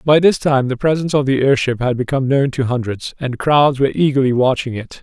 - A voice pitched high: No, low, 135 Hz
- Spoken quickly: Yes, fast, 225 wpm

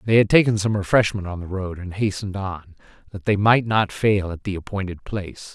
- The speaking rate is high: Yes, fast, 215 wpm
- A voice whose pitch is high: No, low, 100 Hz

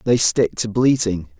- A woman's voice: No, male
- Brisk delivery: No, average, 175 wpm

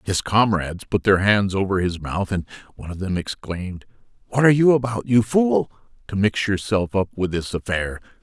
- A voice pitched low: Yes, low, 100 Hz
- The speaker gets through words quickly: No, average, 190 wpm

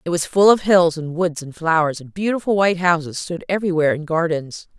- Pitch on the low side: No, medium, 170 Hz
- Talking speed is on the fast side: Yes, fast, 215 wpm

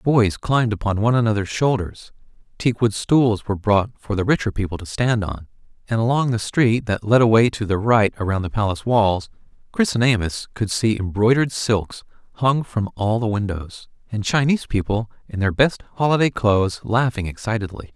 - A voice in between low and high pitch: No, low, 110 Hz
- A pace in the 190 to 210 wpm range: No, average, 175 wpm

